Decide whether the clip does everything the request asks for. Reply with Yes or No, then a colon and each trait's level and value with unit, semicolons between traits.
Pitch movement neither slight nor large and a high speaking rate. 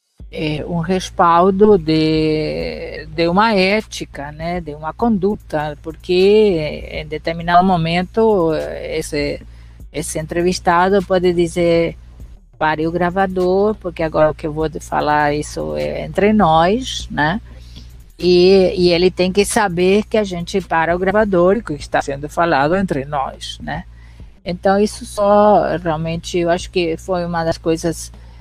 No: average, 3.4 semitones; average, 140 wpm